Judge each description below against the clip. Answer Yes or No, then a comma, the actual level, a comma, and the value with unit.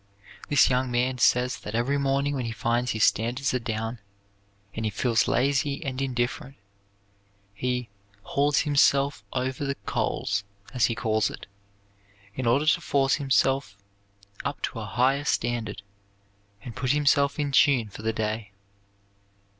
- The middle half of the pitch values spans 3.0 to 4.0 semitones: Yes, average, 3.4 semitones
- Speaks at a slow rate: No, average, 145 wpm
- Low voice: Yes, low, 125 Hz